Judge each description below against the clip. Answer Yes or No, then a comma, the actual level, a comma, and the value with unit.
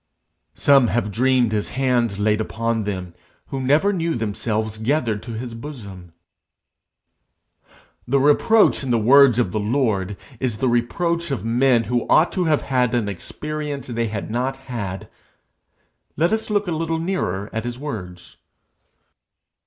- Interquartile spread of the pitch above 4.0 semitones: Yes, average, 4.7 semitones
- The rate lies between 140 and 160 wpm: Yes, average, 150 wpm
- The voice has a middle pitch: No, low, 120 Hz